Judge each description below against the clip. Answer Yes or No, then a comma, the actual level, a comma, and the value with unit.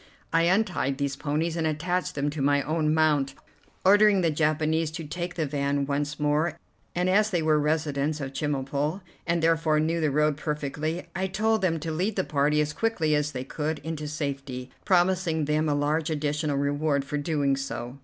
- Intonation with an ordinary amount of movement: No, narrow, 2.3 semitones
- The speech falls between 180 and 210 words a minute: Yes, average, 185 wpm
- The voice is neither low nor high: Yes, medium, 155 Hz